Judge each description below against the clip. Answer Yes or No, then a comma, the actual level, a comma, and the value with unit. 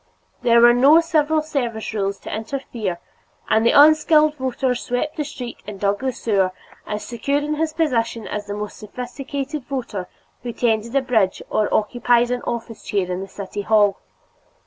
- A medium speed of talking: Yes, average, 170 wpm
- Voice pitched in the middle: No, high, 240 Hz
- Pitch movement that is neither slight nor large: Yes, average, 4.8 semitones